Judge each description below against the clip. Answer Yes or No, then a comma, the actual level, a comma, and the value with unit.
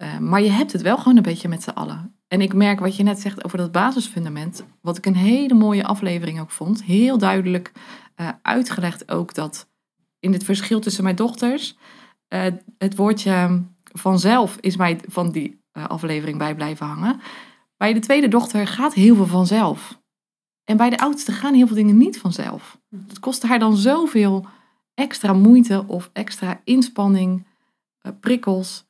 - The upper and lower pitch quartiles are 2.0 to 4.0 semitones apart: No, average, 4.6 semitones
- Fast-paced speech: No, average, 175 wpm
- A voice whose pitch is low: No, high, 205 Hz